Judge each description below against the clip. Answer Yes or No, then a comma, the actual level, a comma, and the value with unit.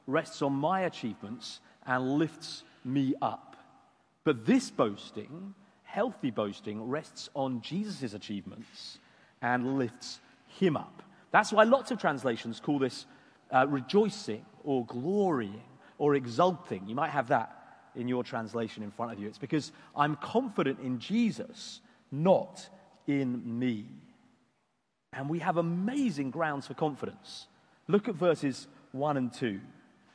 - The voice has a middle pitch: Yes, medium, 145 Hz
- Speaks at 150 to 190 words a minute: No, slow, 135 wpm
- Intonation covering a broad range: Yes, wide, 7.2 semitones